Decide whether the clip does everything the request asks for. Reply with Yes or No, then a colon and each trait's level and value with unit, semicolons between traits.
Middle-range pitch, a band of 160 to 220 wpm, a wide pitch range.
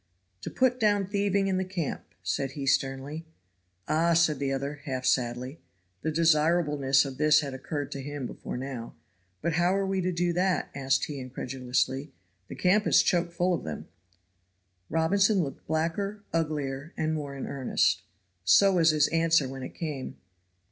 No: medium, 155 Hz; average, 170 wpm; average, 4.5 semitones